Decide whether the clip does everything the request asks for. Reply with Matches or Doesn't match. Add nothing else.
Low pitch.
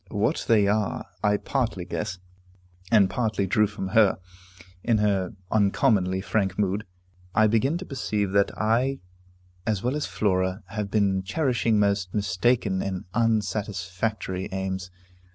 Matches